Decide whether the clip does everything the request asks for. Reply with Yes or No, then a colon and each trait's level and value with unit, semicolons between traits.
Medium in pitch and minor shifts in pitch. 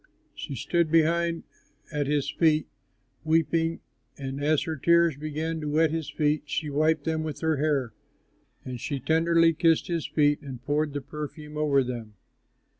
Yes: medium, 155 Hz; narrow, 2.0 semitones